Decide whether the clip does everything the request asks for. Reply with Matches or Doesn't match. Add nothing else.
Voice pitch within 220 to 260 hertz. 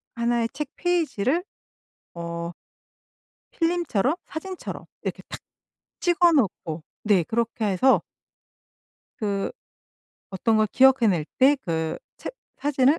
Matches